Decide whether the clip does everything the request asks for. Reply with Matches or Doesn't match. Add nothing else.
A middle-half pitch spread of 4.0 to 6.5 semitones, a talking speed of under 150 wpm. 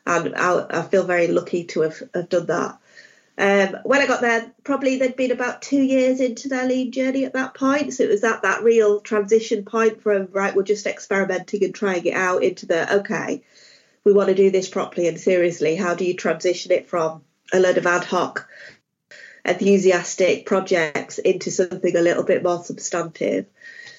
Doesn't match